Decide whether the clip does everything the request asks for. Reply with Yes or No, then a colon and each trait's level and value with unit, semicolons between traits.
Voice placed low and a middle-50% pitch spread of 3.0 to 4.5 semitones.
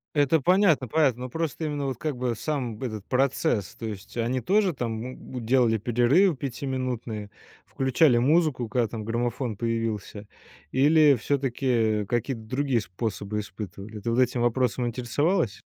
Yes: low, 125 Hz; average, 3.7 semitones